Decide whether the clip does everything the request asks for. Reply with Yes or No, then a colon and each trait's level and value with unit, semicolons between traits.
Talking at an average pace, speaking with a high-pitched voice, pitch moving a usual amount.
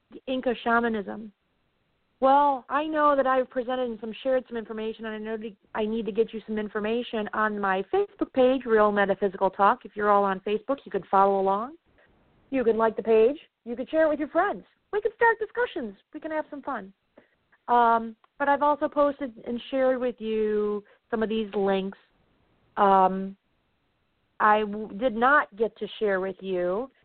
Yes: average, 185 wpm; high, 225 Hz; average, 4.1 semitones